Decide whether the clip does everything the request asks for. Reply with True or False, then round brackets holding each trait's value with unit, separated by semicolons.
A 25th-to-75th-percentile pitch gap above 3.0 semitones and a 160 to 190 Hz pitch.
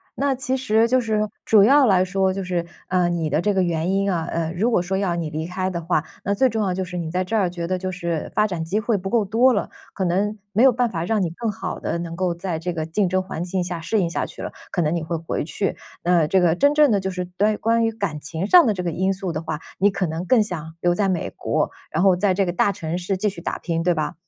True (3.4 semitones; 185 Hz)